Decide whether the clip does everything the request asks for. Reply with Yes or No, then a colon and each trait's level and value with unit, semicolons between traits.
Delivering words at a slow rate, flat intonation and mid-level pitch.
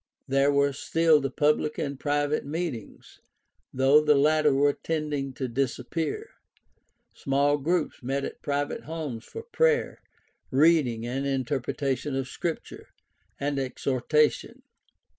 Yes: slow, 120 wpm; narrow, 2.2 semitones; medium, 145 Hz